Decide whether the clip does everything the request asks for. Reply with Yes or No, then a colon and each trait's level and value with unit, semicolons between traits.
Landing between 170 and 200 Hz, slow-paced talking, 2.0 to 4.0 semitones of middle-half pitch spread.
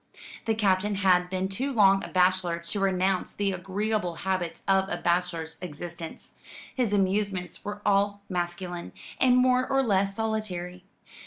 No: high, 190 Hz; average, 145 wpm; narrow, 2.5 semitones